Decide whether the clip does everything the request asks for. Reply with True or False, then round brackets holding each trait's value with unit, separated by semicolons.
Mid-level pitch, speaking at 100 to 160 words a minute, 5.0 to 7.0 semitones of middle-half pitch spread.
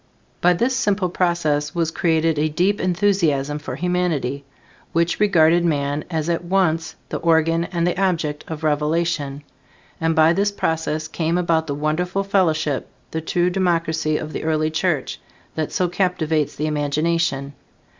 False (165 Hz; 150 wpm; 2.5 semitones)